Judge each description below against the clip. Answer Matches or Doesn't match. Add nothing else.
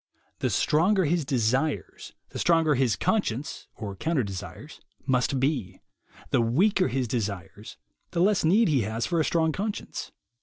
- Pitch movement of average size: Doesn't match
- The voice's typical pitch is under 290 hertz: Matches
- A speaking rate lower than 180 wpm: Matches